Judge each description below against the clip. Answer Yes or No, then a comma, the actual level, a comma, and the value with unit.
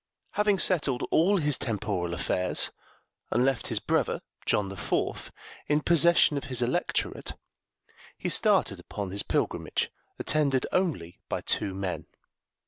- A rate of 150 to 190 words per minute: No, slow, 135 wpm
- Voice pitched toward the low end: Yes, low, 130 Hz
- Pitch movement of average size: No, wide, 8.2 semitones